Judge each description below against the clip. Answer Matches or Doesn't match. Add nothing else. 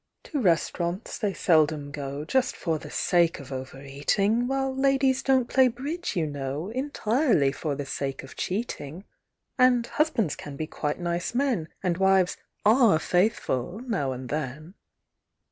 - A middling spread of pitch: Doesn't match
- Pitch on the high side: Doesn't match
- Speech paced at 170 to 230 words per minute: Doesn't match